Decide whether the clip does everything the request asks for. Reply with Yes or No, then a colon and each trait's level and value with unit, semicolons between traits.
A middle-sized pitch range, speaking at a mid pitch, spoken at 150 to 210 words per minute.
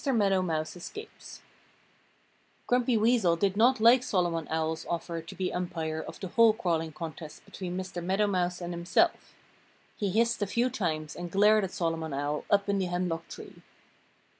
Yes: average, 4.2 semitones; medium, 180 Hz; average, 165 wpm